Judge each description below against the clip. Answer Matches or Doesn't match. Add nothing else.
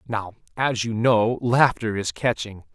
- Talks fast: Doesn't match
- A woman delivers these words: Doesn't match